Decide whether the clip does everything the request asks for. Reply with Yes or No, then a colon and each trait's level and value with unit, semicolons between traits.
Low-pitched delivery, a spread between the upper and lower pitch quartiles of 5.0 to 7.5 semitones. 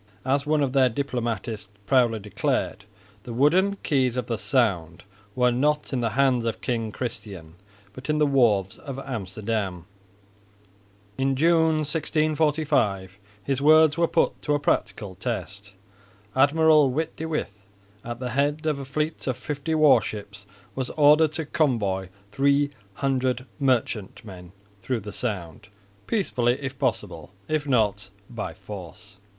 Yes: low, 130 Hz; wide, 5.6 semitones